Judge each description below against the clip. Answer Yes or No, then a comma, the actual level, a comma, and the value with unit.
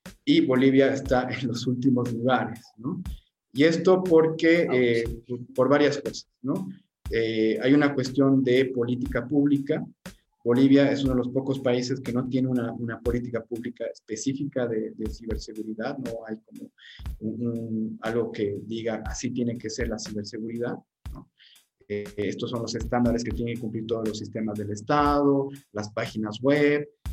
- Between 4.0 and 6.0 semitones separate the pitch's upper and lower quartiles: No, average, 3.3 semitones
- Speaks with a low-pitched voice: Yes, low, 120 Hz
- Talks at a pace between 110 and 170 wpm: Yes, average, 160 wpm